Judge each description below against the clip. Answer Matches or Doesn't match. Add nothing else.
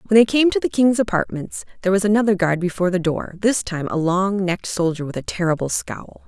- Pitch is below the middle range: Doesn't match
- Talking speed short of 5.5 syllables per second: Doesn't match